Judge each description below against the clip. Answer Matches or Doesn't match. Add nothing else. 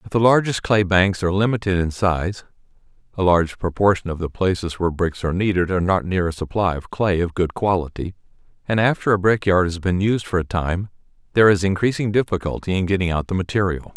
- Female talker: Doesn't match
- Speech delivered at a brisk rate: Matches